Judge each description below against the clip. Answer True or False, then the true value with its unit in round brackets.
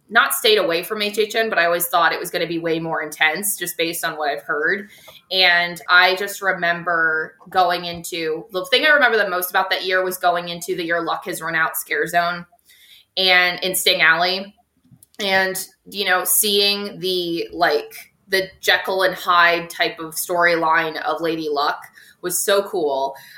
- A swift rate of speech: False (185 wpm)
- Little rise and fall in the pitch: True (2.2 semitones)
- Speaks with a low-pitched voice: False (180 Hz)